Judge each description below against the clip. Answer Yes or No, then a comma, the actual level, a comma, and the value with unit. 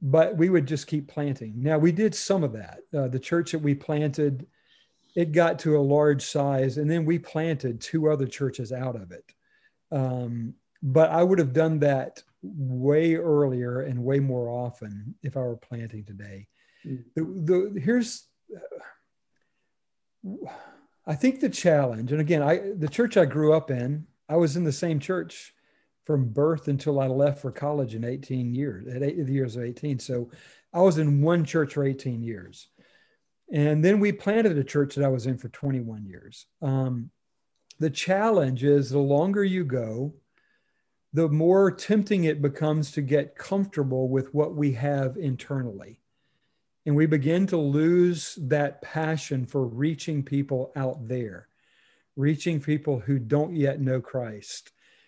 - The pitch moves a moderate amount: Yes, average, 3.9 semitones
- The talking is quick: No, average, 165 wpm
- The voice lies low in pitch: No, medium, 145 Hz